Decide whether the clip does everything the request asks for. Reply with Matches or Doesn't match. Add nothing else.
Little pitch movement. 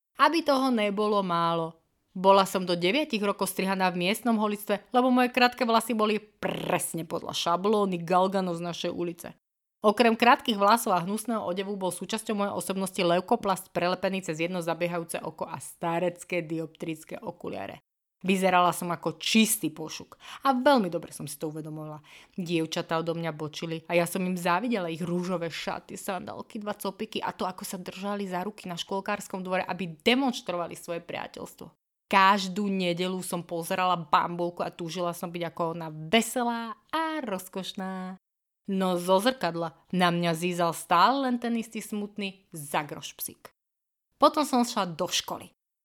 Doesn't match